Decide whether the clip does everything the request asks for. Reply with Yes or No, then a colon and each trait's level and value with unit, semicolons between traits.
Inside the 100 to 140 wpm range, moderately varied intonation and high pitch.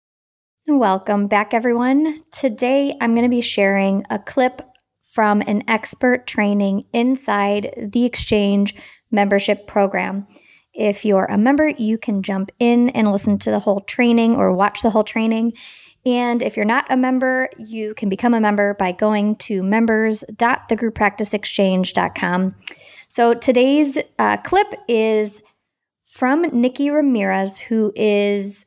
Yes: slow, 135 wpm; average, 3.3 semitones; high, 220 Hz